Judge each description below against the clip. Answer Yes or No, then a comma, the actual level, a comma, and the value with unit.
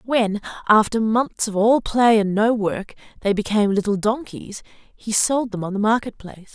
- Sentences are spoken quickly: No, average, 185 wpm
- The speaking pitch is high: Yes, high, 215 Hz